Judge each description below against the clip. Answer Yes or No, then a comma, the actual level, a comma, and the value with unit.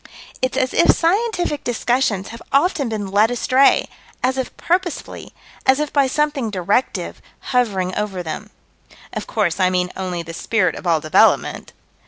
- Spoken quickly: No, average, 155 wpm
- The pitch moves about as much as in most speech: No, wide, 6.5 semitones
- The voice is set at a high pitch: Yes, high, 230 Hz